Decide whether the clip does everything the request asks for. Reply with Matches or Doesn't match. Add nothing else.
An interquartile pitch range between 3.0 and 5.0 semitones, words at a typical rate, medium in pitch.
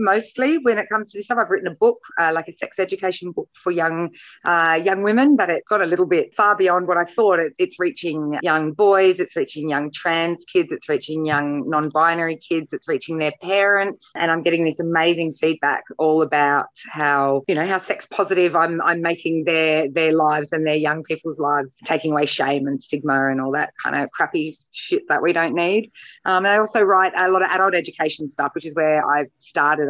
Doesn't match